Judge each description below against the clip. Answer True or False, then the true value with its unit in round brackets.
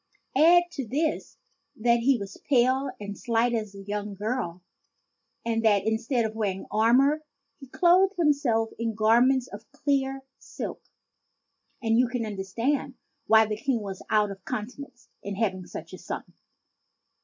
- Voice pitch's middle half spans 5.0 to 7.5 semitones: False (4.2 semitones)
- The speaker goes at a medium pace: True (155 wpm)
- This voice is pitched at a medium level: False (230 Hz)